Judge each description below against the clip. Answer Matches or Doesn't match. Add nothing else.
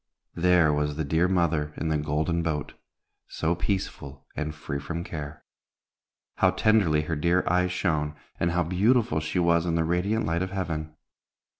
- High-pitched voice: Doesn't match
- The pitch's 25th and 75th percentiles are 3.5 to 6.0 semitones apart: Doesn't match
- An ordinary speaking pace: Matches